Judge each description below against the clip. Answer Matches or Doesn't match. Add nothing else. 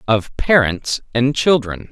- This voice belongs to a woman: Doesn't match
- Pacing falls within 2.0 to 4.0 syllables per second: Matches